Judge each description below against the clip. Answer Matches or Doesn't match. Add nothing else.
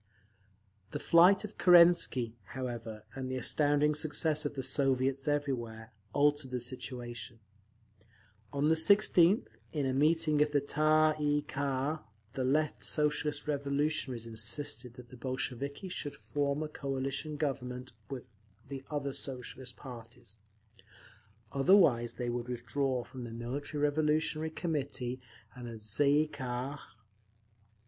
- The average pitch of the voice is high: Doesn't match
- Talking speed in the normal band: Doesn't match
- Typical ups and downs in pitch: Matches